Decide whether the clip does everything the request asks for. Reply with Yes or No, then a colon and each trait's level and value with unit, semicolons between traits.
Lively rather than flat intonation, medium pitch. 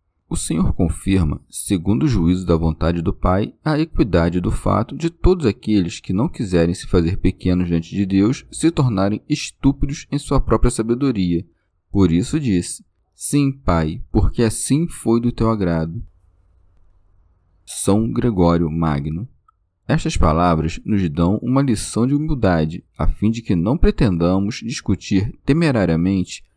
No: wide, 6.1 semitones; very low, 95 Hz